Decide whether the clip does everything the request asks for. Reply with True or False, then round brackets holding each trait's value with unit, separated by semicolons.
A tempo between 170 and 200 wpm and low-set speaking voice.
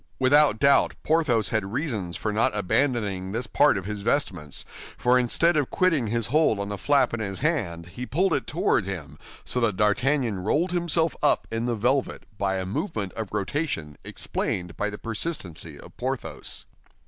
True (175 wpm; 115 Hz)